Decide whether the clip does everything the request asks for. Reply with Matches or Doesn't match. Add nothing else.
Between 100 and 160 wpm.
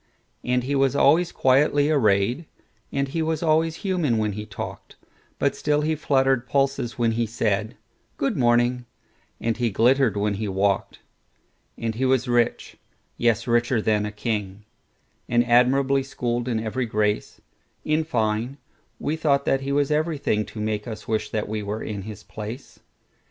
Matches